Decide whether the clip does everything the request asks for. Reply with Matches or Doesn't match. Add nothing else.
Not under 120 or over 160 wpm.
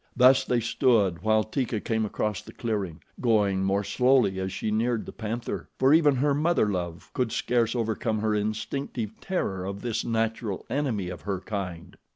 Doesn't match